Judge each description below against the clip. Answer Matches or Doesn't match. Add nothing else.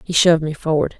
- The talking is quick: Matches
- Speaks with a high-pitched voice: Doesn't match